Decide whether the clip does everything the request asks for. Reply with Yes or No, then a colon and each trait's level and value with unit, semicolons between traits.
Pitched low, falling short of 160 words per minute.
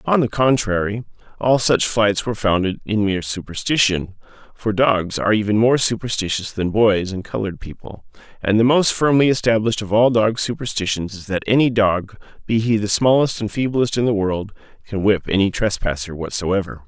No: low, 105 Hz; average, 165 wpm